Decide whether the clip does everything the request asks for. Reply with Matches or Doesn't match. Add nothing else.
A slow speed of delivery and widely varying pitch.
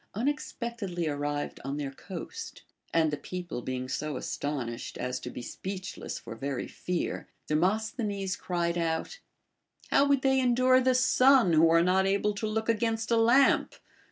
Doesn't match